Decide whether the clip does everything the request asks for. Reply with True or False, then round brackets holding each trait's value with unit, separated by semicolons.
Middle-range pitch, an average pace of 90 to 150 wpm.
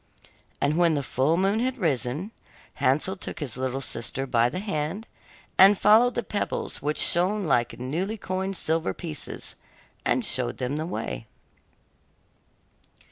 True (165 Hz; 140 wpm)